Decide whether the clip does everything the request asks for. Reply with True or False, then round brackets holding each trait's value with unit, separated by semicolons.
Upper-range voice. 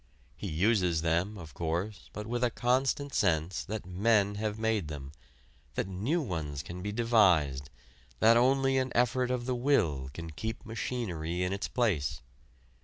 False (105 Hz)